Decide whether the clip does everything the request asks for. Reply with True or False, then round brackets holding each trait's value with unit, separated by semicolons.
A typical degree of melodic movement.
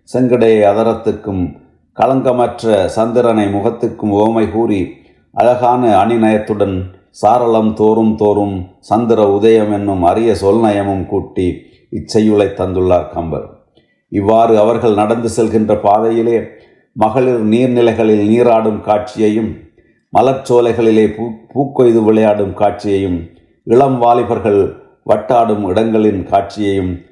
False (2.2 semitones)